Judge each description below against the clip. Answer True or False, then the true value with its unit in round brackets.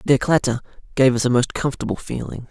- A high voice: False (130 Hz)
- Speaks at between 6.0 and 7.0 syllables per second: True (6.4 syllables/s)